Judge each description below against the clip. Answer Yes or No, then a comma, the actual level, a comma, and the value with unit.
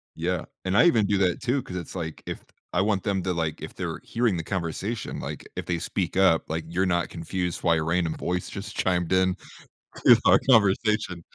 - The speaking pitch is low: Yes, very low, 90 Hz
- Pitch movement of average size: Yes, average, 3.0 semitones